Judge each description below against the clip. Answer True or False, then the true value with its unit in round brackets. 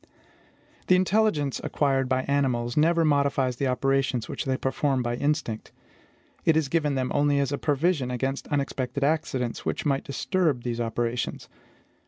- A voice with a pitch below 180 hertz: True (135 Hz)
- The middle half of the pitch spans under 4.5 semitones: True (2.7 semitones)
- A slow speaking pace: False (150 wpm)